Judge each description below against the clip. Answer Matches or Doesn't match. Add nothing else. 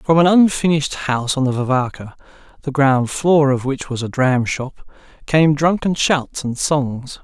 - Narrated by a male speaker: Matches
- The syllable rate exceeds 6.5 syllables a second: Doesn't match